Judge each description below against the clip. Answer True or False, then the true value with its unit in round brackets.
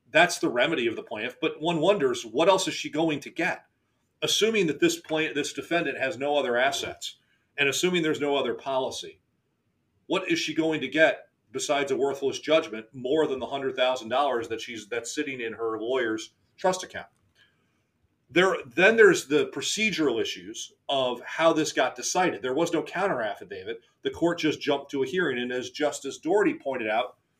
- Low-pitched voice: False (155 Hz)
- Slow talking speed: False (190 wpm)